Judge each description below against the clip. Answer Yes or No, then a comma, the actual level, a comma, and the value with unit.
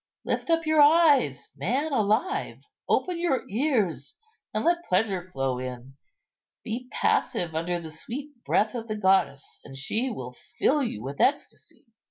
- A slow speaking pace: No, average, 150 wpm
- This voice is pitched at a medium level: No, high, 215 Hz